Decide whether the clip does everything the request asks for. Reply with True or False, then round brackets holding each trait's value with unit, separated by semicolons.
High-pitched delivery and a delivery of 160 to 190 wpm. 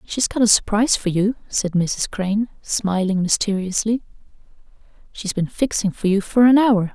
True (205 Hz; 165 wpm)